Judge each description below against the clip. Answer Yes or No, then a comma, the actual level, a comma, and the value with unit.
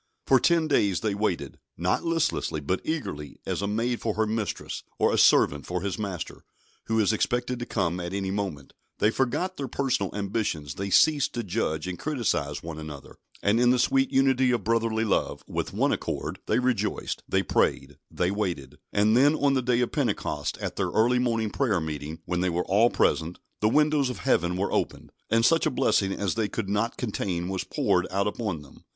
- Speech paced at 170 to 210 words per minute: Yes, average, 200 wpm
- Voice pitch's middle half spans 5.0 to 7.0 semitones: Yes, average, 5.3 semitones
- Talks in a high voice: No, low, 105 Hz